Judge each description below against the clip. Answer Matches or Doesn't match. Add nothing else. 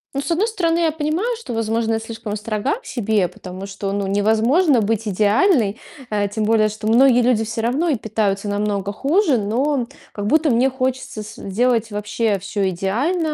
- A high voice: Matches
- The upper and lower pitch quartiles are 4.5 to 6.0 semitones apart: Matches